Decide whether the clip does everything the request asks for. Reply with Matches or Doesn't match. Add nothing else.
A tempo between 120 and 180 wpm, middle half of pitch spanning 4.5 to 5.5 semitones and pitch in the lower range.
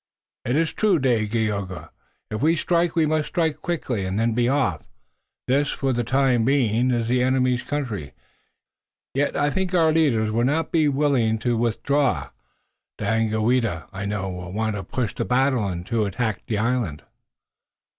Matches